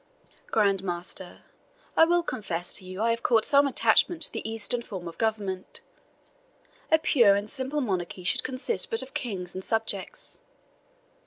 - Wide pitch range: Yes, wide, 5.7 semitones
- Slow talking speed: No, average, 160 wpm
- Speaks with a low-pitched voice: No, high, 220 Hz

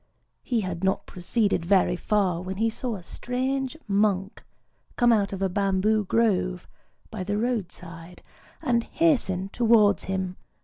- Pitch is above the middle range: Yes, high, 200 Hz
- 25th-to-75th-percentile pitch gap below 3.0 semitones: No, average, 3.8 semitones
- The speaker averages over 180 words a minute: No, average, 145 wpm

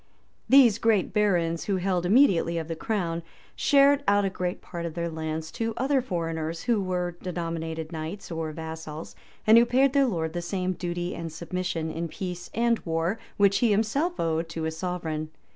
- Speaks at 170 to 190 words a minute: Yes, average, 180 wpm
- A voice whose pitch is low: No, medium, 175 Hz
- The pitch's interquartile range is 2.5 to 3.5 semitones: No, average, 4.2 semitones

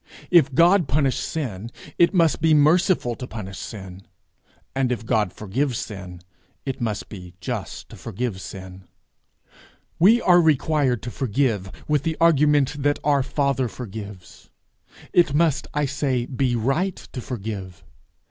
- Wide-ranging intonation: Yes, wide, 5.9 semitones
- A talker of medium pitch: No, low, 130 Hz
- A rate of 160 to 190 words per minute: No, average, 140 wpm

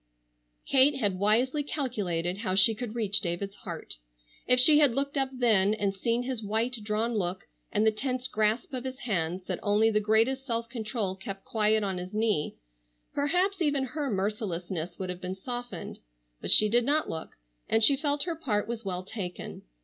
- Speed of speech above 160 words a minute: Yes, average, 185 wpm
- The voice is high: Yes, high, 220 Hz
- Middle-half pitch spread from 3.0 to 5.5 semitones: Yes, average, 4.6 semitones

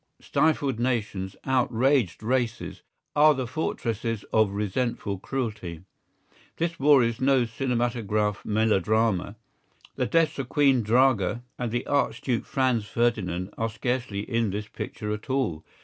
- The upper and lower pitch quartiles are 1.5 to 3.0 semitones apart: No, average, 3.7 semitones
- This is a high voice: No, low, 115 Hz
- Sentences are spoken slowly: Yes, slow, 125 wpm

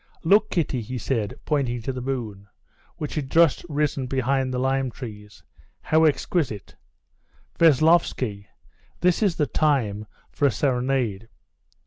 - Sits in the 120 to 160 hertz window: Yes, low, 135 Hz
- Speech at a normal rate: No, slow, 125 wpm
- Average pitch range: Yes, average, 4.5 semitones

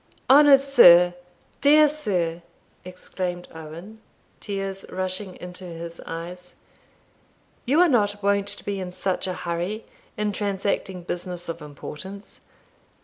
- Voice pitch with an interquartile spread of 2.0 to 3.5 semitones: Yes, average, 2.8 semitones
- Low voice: No, medium, 185 Hz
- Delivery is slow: Yes, slow, 120 wpm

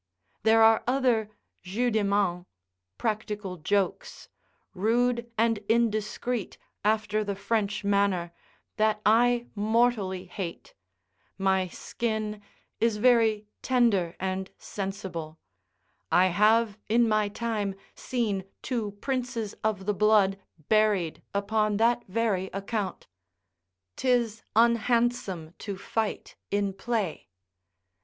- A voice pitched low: No, high, 215 Hz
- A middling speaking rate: No, slow, 105 wpm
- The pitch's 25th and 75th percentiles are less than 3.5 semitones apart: Yes, average, 2.8 semitones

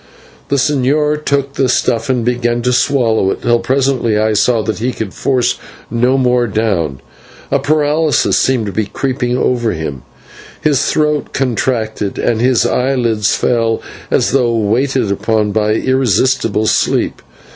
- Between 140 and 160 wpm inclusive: Yes, average, 150 wpm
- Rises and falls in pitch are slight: No, average, 3.2 semitones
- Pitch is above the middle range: No, low, 120 Hz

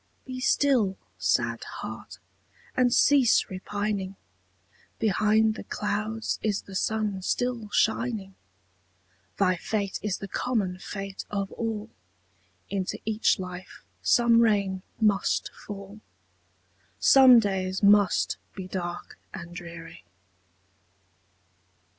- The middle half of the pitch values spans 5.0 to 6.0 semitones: No, narrow, 2.6 semitones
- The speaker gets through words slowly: Yes, slow, 100 wpm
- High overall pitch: Yes, high, 205 Hz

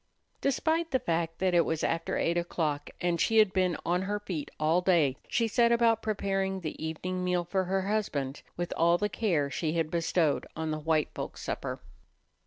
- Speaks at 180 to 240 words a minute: Yes, average, 195 wpm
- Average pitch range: Yes, average, 3.7 semitones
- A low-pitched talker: No, medium, 175 Hz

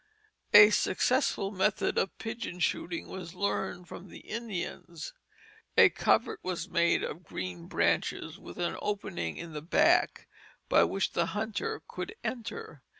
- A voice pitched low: No, medium, 185 Hz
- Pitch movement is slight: No, average, 3.6 semitones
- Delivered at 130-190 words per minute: Yes, average, 140 wpm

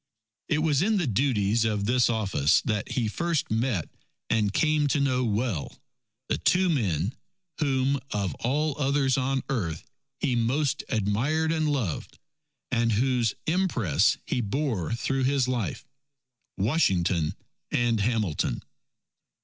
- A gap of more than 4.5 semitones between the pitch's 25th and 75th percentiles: Yes, average, 5.2 semitones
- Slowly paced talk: Yes, slow, 130 wpm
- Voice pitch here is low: Yes, low, 125 Hz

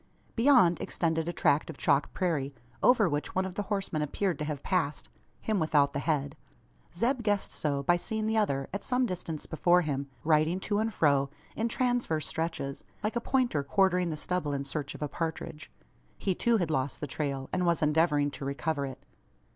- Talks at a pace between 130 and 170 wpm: No, average, 195 wpm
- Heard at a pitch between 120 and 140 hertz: No, medium, 160 Hz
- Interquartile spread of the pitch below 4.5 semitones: No, average, 5.3 semitones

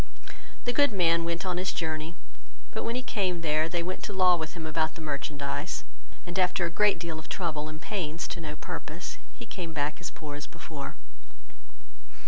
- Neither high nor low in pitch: Yes, medium, 165 Hz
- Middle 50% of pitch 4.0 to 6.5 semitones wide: No, average, 2.8 semitones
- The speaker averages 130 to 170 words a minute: No, average, 195 wpm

